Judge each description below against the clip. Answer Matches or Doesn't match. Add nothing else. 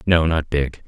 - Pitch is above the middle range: Doesn't match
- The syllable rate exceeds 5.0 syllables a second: Doesn't match